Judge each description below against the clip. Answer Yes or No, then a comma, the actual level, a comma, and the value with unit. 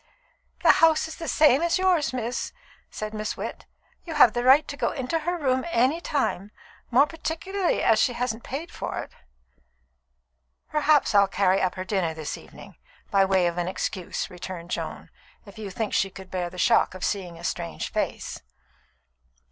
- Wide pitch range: Yes, wide, 8.1 semitones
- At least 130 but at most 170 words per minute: No, average, 180 wpm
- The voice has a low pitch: No, high, 230 Hz